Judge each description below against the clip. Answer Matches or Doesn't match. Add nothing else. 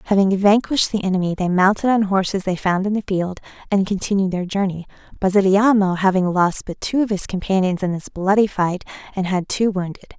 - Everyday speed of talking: Matches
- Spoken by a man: Doesn't match